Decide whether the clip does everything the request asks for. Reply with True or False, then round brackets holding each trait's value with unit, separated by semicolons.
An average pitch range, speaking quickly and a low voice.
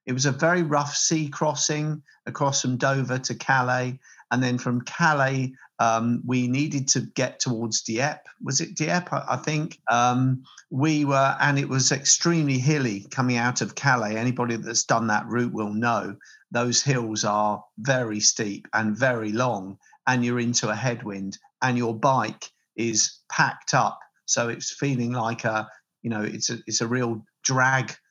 False (3.0 semitones; 170 wpm; 125 Hz)